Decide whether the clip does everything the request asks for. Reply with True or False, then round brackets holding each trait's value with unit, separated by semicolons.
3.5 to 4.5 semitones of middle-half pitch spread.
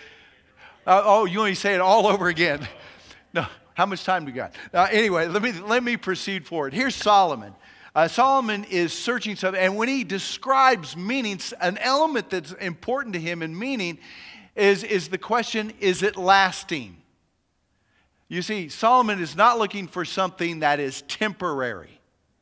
True (3.9 semitones)